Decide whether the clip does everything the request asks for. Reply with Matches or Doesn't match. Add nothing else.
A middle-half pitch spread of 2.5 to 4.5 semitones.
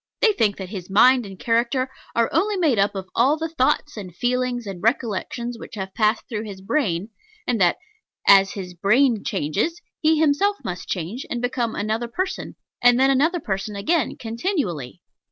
Doesn't match